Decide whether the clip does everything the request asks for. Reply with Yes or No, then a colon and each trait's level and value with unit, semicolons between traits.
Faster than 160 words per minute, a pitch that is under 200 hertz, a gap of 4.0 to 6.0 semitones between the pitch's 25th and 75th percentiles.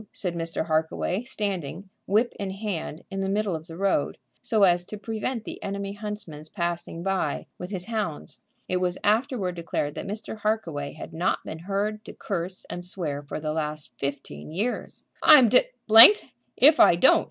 Yes: average, 175 wpm; high, 190 Hz; average, 4.3 semitones